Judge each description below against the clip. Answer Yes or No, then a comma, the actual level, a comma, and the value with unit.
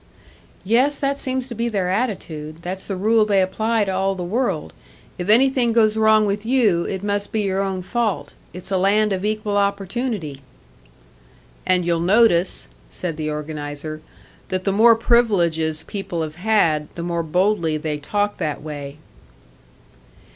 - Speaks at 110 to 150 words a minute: No, average, 160 wpm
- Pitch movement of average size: Yes, average, 4.4 semitones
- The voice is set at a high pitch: Yes, high, 195 Hz